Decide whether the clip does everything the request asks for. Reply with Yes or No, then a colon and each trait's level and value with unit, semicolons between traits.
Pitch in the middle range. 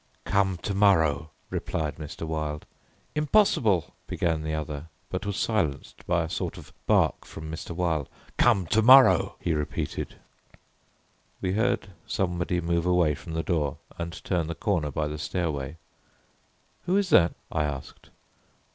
No: very low, 85 Hz